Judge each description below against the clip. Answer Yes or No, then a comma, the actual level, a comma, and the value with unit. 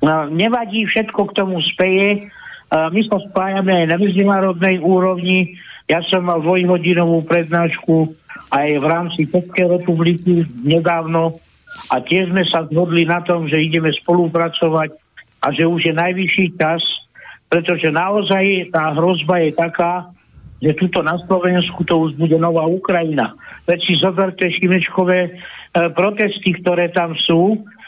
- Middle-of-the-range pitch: Yes, medium, 175 Hz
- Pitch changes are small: Yes, narrow, 2.0 semitones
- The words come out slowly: No, average, 135 wpm